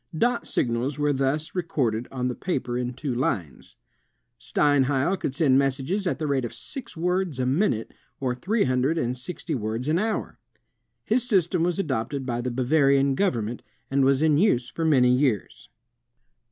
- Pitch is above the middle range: No, low, 135 Hz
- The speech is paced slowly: No, average, 170 wpm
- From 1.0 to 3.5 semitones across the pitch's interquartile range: No, average, 4.8 semitones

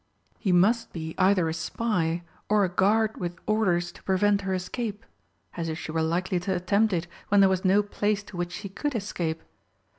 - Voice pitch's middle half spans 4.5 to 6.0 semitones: No, average, 3.0 semitones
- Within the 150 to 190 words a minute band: No, average, 200 wpm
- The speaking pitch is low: No, high, 190 Hz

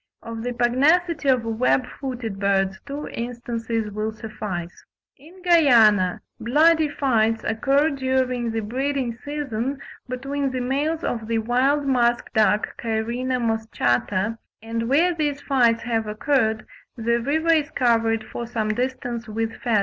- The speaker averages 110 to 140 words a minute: Yes, slow, 135 wpm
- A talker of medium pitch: No, high, 240 Hz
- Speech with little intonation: No, average, 3.7 semitones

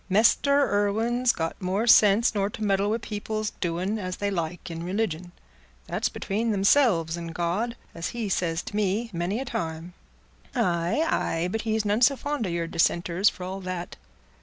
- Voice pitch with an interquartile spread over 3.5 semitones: Yes, average, 4.3 semitones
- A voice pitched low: No, high, 195 Hz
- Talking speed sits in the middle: Yes, average, 175 wpm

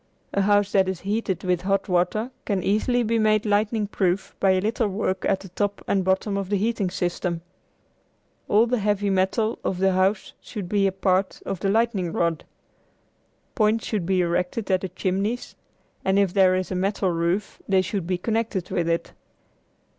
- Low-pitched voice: No, high, 195 Hz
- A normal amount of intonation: No, narrow, 2.2 semitones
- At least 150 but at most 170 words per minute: No, average, 185 wpm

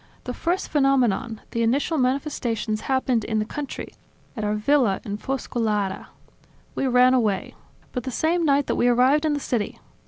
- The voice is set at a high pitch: Yes, very high, 250 Hz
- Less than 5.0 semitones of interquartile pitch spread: Yes, average, 4.1 semitones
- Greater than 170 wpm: No, average, 165 wpm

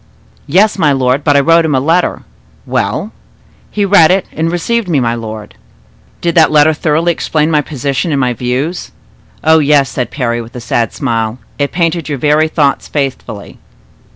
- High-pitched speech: No, medium, 150 Hz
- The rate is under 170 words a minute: No, average, 180 wpm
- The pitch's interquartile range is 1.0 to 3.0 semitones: No, average, 4.3 semitones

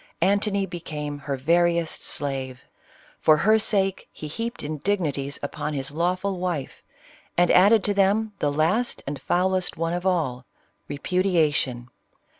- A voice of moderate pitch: Yes, medium, 170 Hz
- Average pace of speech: No, slow, 130 wpm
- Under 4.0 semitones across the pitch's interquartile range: No, average, 4.9 semitones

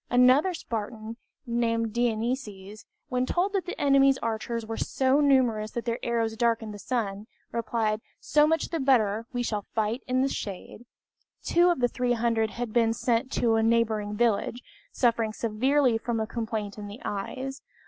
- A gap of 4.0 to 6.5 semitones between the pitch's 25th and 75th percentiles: No, average, 2.7 semitones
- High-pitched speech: Yes, high, 230 Hz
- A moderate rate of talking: Yes, average, 165 wpm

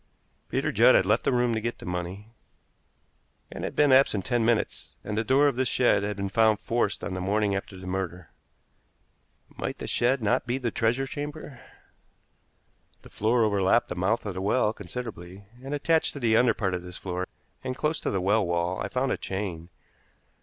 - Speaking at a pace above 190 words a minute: Yes, average, 200 wpm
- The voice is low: Yes, low, 110 Hz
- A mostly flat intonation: No, average, 4.7 semitones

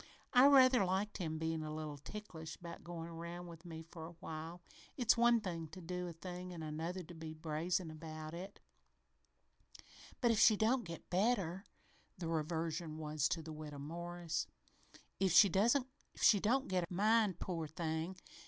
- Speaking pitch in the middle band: Yes, medium, 170 Hz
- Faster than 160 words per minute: Yes, average, 170 wpm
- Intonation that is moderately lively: Yes, average, 3.2 semitones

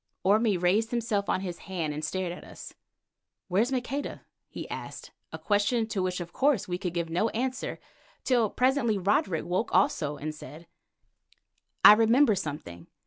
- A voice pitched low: No, high, 195 Hz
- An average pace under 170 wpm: Yes, average, 160 wpm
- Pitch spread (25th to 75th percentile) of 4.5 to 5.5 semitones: Yes, average, 4.9 semitones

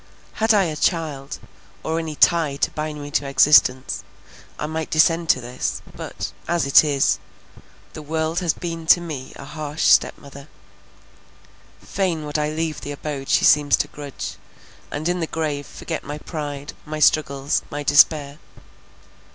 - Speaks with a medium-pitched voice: Yes, medium, 150 Hz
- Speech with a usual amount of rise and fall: No, narrow, 2.2 semitones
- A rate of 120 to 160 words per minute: Yes, average, 155 wpm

